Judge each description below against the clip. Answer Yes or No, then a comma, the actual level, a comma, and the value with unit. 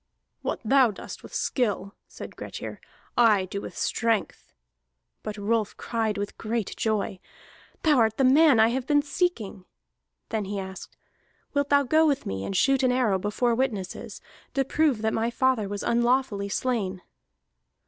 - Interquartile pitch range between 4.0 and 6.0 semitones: Yes, average, 4.3 semitones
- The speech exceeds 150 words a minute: Yes, average, 160 wpm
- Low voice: No, high, 230 Hz